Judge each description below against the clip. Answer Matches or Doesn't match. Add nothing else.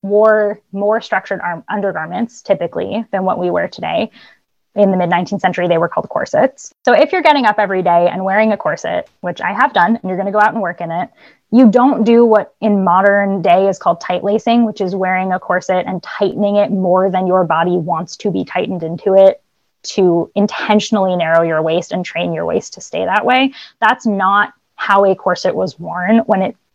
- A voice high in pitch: Matches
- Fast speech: Matches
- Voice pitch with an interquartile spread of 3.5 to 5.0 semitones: Doesn't match